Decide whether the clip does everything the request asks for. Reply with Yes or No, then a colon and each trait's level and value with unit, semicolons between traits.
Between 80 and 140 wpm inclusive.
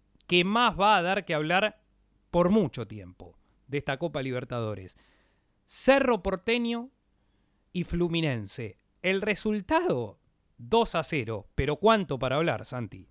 Yes: average, 130 wpm